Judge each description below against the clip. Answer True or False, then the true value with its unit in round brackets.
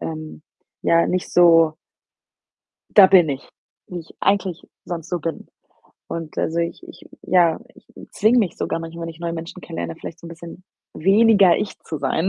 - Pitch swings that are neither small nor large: False (2.2 semitones)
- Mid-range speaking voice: True (170 Hz)